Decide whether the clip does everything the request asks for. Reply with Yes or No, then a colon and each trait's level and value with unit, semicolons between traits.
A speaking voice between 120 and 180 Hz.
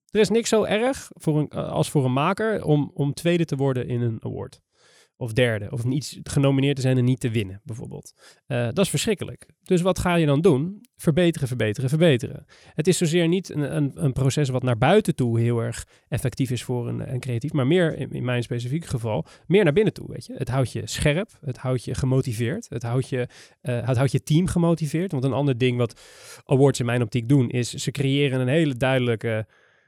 Yes: low, 135 Hz